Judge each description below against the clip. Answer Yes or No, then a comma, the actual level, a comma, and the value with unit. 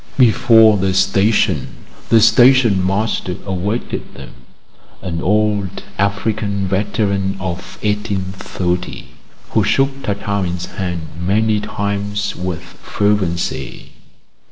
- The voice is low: Yes, low, 100 Hz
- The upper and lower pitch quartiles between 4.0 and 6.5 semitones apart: No, narrow, 2.4 semitones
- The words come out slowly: Yes, slow, 90 wpm